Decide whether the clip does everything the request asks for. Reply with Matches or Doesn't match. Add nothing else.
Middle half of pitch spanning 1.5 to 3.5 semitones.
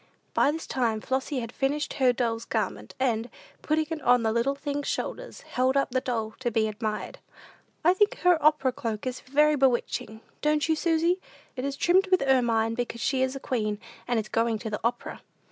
Doesn't match